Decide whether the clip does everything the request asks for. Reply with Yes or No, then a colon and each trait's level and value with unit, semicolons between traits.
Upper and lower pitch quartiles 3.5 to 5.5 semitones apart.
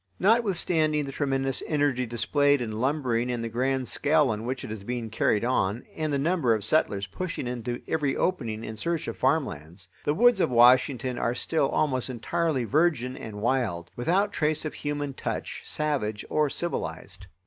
Yes: average, 4.8 semitones